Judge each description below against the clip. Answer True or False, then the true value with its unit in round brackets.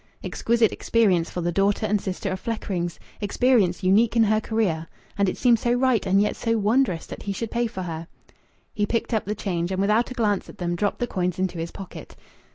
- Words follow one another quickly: True (220 wpm)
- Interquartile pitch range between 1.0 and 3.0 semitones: False (3.8 semitones)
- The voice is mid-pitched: False (205 Hz)